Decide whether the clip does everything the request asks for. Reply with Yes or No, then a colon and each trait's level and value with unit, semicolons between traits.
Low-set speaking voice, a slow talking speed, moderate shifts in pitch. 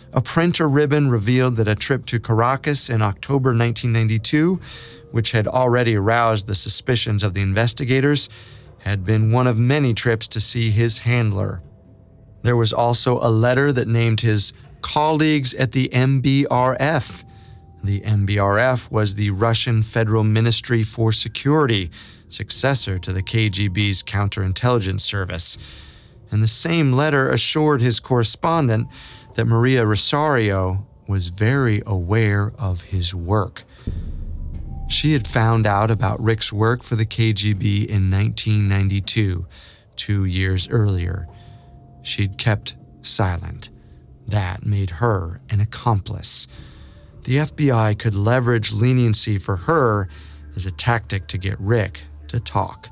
Yes: low, 110 Hz; slow, 125 wpm; average, 3.7 semitones